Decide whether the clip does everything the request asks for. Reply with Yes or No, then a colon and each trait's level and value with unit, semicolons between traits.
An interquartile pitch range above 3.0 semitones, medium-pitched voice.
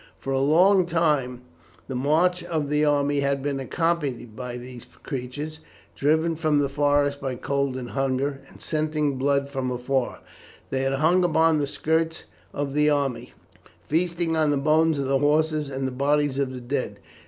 No: narrow, 2.6 semitones; medium, 145 Hz